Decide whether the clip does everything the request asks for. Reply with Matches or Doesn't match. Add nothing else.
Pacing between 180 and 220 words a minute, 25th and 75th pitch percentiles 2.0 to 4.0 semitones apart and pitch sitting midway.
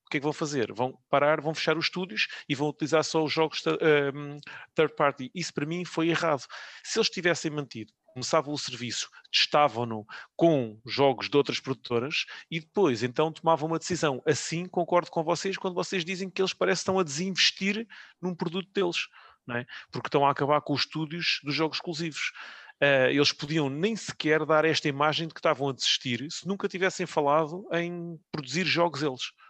Matches